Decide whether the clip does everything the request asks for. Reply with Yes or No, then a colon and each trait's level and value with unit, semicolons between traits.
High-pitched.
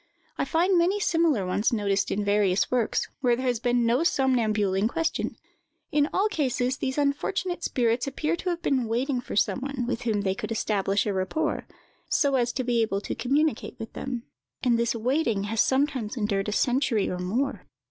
Yes: high, 245 Hz